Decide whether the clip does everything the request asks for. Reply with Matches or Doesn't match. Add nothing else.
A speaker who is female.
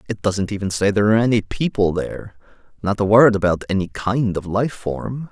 Doesn't match